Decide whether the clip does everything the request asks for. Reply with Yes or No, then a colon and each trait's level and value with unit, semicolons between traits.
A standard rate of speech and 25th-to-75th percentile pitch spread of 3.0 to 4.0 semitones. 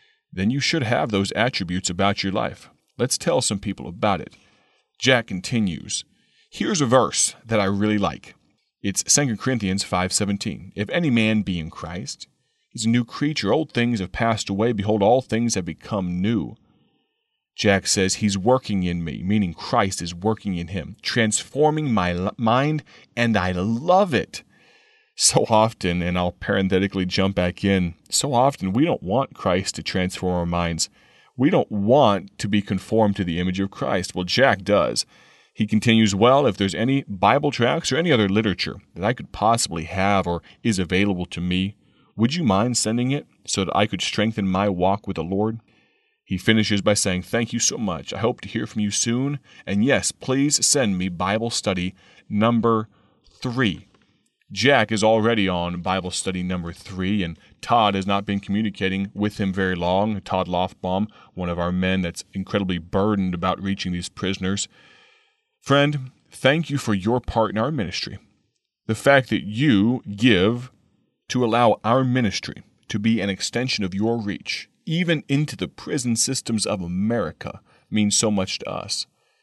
Yes: average, 175 wpm; average, 3.7 semitones